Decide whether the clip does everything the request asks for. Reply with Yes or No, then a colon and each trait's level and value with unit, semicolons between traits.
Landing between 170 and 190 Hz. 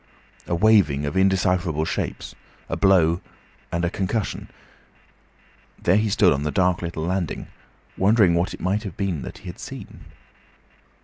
No: very low, 90 Hz